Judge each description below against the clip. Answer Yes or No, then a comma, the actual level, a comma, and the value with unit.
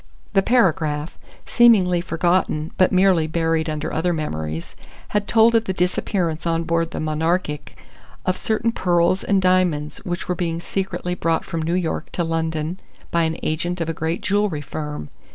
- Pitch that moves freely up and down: No, average, 2.7 semitones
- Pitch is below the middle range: No, medium, 170 Hz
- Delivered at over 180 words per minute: No, average, 165 wpm